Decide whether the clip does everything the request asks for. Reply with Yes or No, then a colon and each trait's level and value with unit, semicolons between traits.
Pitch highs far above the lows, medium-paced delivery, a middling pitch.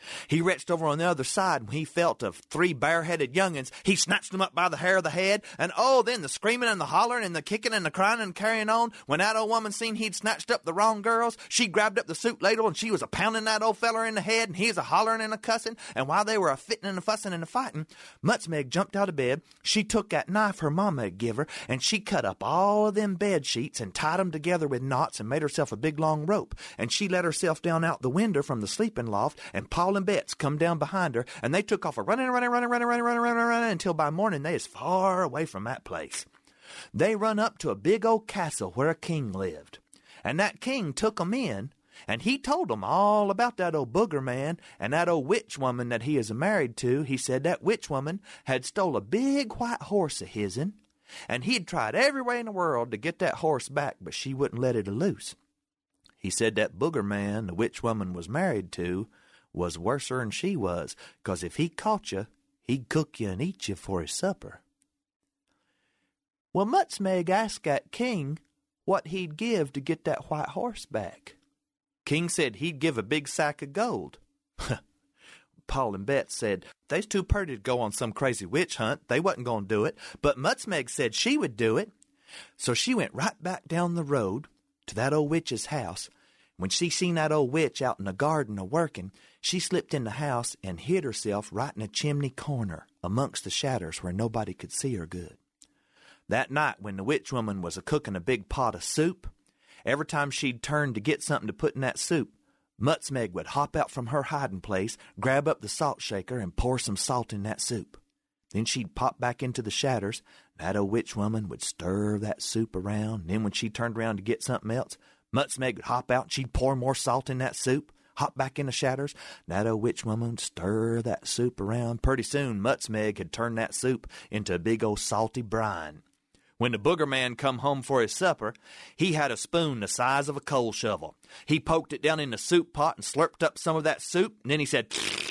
No: wide, 8.8 semitones; fast, 225 wpm; medium, 150 Hz